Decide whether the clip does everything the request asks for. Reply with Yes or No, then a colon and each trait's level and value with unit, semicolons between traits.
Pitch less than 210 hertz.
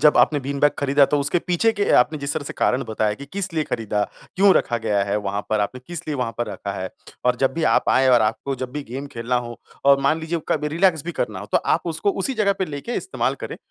Yes: medium, 140 Hz